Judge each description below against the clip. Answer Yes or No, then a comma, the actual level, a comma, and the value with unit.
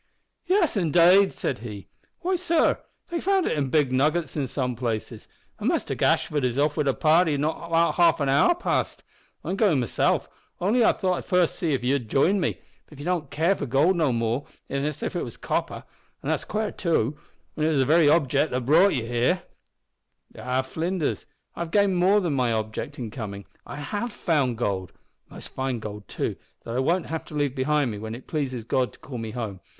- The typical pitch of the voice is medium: Yes, medium, 145 Hz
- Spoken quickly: Yes, fast, 215 wpm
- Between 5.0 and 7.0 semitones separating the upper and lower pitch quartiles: Yes, wide, 5.5 semitones